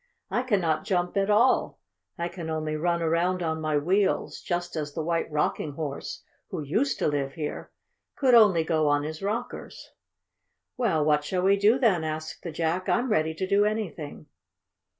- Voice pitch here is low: No, medium, 170 Hz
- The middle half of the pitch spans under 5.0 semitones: Yes, average, 4.2 semitones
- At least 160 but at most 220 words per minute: Yes, average, 175 wpm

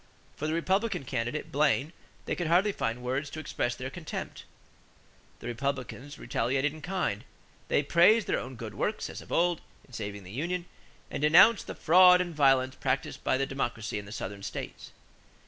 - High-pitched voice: No, medium, 140 Hz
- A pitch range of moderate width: No, wide, 5.8 semitones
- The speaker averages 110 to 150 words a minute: No, average, 180 wpm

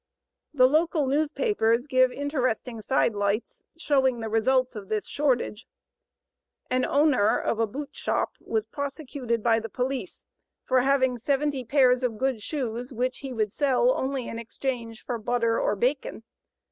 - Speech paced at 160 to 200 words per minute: No, average, 150 wpm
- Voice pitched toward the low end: No, very high, 255 Hz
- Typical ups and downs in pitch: Yes, average, 3.4 semitones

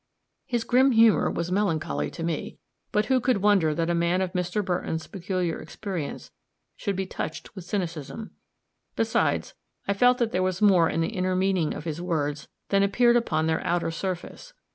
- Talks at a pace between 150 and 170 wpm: No, average, 180 wpm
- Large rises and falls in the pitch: No, average, 3.9 semitones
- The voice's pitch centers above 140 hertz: Yes, medium, 185 Hz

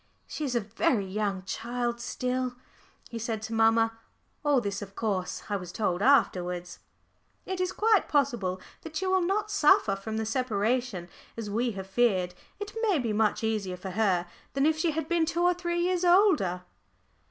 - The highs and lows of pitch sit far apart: Yes, wide, 7.9 semitones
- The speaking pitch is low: No, high, 230 Hz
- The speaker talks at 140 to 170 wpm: No, average, 180 wpm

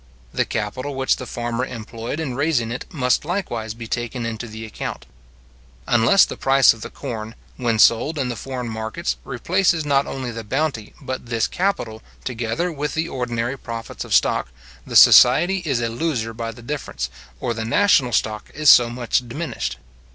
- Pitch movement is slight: No, average, 3.9 semitones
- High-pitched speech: No, low, 120 Hz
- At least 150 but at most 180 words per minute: Yes, average, 175 wpm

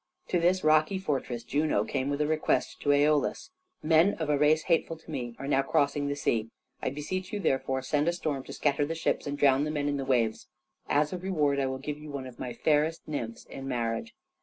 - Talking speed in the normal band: No, fast, 230 wpm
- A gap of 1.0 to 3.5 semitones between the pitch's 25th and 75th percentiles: Yes, average, 2.7 semitones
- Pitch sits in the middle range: Yes, medium, 145 Hz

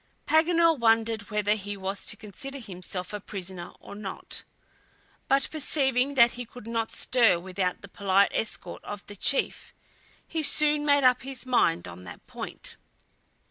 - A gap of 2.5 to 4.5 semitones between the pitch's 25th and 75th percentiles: No, wide, 5.5 semitones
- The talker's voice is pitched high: Yes, high, 225 Hz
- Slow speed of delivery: No, average, 155 wpm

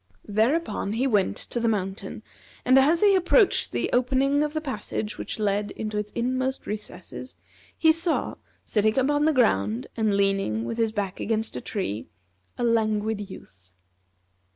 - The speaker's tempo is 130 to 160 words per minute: Yes, average, 155 wpm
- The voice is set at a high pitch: Yes, high, 220 Hz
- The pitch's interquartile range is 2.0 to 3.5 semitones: No, average, 4.7 semitones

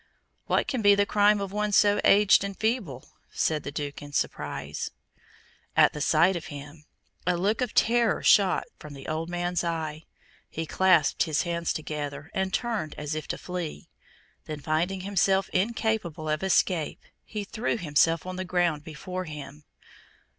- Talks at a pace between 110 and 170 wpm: Yes, average, 165 wpm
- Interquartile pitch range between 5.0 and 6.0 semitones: No, average, 4.6 semitones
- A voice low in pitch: No, medium, 175 Hz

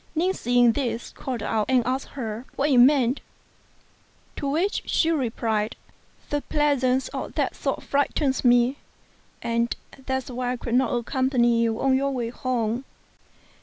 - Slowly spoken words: No, average, 155 wpm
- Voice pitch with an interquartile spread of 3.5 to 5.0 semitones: No, narrow, 2.6 semitones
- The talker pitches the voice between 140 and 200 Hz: No, very high, 255 Hz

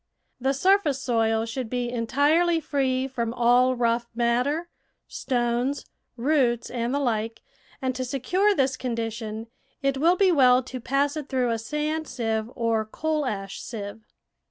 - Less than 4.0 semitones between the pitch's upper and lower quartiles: Yes, average, 3.5 semitones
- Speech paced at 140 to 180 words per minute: Yes, average, 150 wpm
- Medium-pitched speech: No, very high, 255 Hz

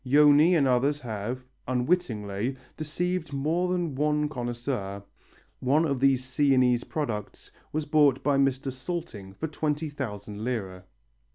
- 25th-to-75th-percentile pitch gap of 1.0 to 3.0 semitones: No, average, 3.7 semitones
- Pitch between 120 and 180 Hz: Yes, low, 135 Hz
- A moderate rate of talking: No, slow, 125 wpm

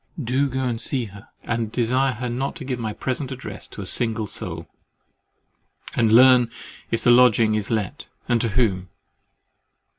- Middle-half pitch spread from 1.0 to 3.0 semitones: Yes, average, 2.7 semitones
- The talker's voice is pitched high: No, low, 120 Hz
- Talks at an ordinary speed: Yes, average, 170 wpm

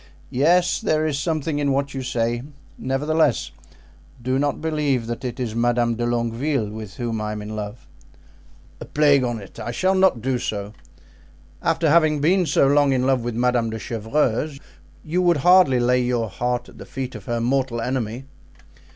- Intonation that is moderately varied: Yes, average, 3.9 semitones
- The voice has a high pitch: No, low, 130 Hz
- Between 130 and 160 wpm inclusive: No, average, 175 wpm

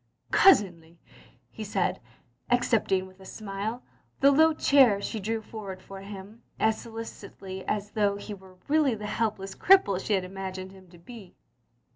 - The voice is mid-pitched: No, high, 200 Hz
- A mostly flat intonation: No, average, 3.1 semitones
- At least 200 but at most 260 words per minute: No, average, 160 wpm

